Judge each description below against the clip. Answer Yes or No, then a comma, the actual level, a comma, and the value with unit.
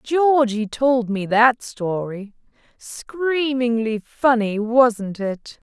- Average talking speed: No, slow, 95 wpm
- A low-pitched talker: No, high, 240 Hz